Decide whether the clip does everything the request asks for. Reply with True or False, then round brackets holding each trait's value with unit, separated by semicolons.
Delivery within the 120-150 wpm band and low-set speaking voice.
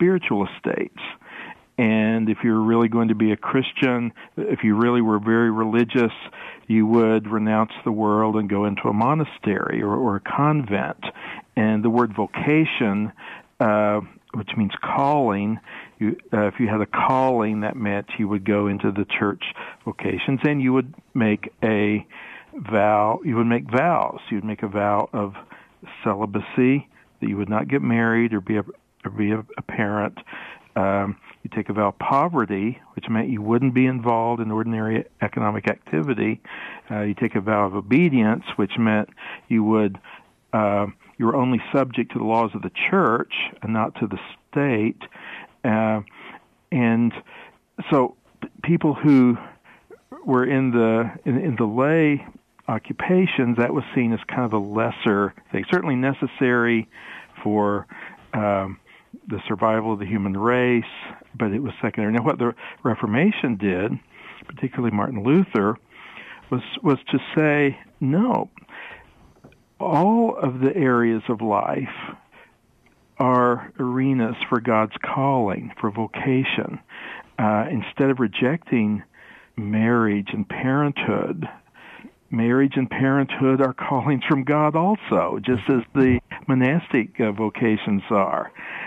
True (145 wpm; 115 Hz)